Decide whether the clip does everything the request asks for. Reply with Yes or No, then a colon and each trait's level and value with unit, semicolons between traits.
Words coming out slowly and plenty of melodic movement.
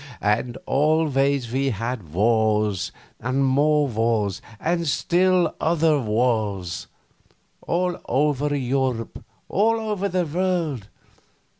Yes: slow, 100 wpm; wide, 6.1 semitones